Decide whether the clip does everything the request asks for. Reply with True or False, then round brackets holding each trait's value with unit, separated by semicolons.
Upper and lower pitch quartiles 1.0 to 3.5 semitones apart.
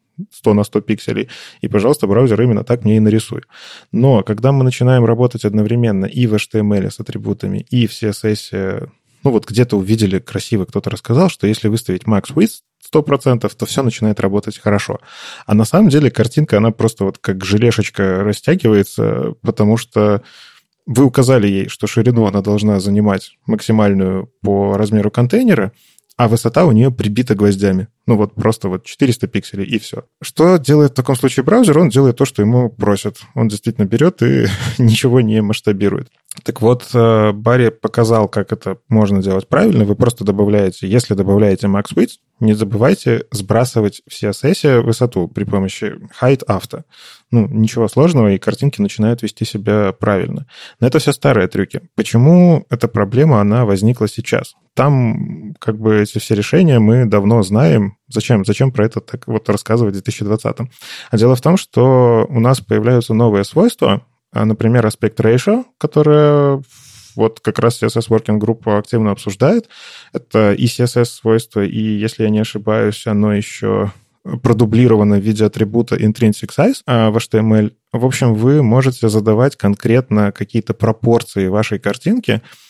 True (3.1 semitones)